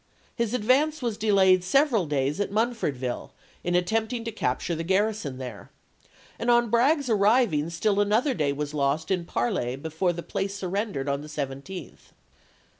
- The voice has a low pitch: No, high, 190 Hz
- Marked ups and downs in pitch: Yes, wide, 7.1 semitones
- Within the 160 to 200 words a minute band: Yes, average, 165 wpm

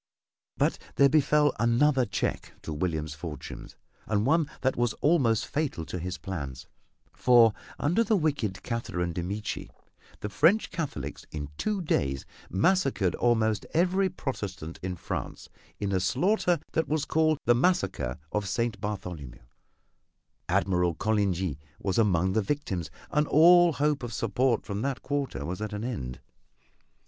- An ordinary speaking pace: Yes, average, 145 wpm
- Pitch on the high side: No, low, 110 Hz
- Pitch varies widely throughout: Yes, wide, 8.2 semitones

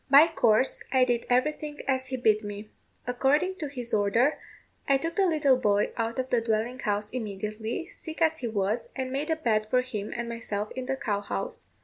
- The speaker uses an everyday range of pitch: Yes, average, 4.5 semitones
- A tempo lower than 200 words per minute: No, fast, 205 wpm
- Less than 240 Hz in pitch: No, very high, 250 Hz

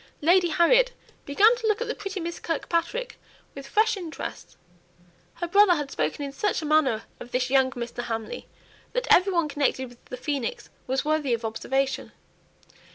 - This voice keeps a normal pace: Yes, average, 170 wpm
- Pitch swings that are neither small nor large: No, wide, 6.8 semitones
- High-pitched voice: Yes, very high, 310 Hz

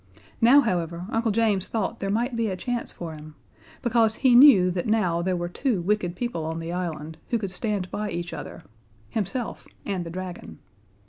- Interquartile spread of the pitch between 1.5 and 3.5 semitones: No, average, 4.7 semitones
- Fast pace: No, average, 190 wpm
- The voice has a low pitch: No, high, 190 Hz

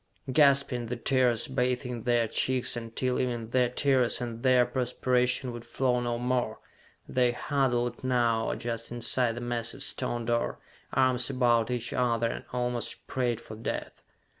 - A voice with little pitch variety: Yes, narrow, 1.3 semitones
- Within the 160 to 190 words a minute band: No, average, 145 wpm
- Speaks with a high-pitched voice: No, low, 125 Hz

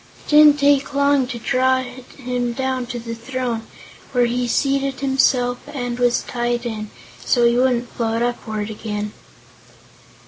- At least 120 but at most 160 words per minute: Yes, average, 145 wpm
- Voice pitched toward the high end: Yes, high, 245 Hz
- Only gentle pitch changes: Yes, narrow, 1.9 semitones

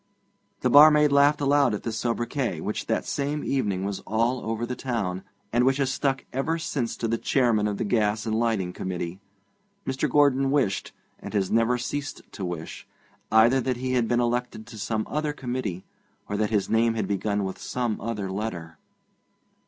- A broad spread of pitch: No, average, 4.3 semitones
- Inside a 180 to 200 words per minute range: Yes, average, 185 wpm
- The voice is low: Yes, low, 115 Hz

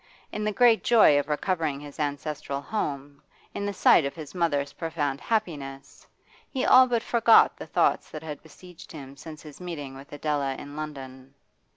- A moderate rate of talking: Yes, average, 175 wpm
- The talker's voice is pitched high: No, medium, 150 Hz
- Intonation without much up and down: No, average, 4.2 semitones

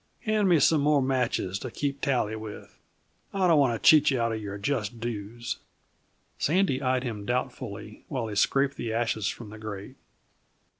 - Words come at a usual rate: Yes, average, 180 wpm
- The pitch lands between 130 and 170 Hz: No, low, 120 Hz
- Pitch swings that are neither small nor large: Yes, average, 4.4 semitones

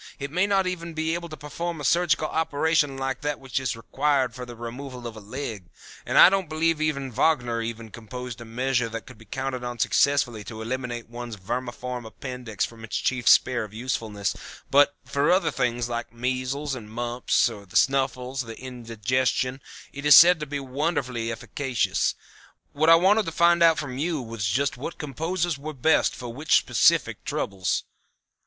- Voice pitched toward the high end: No, low, 130 Hz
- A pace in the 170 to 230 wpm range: Yes, average, 175 wpm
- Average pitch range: Yes, average, 4.1 semitones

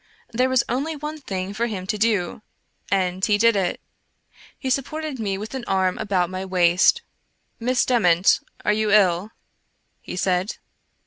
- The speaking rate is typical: Yes, average, 170 wpm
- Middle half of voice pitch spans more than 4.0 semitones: Yes, average, 4.7 semitones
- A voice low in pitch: No, high, 205 Hz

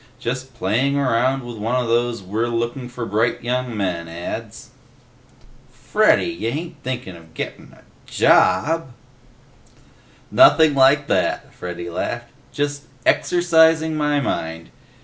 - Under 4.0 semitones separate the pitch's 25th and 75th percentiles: No, average, 5.0 semitones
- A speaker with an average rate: No, slow, 120 wpm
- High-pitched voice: No, low, 120 Hz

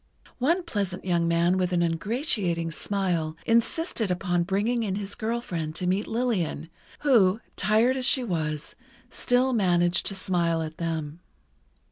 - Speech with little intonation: No, average, 5.3 semitones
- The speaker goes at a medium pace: Yes, average, 145 wpm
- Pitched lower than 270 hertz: Yes, medium, 185 Hz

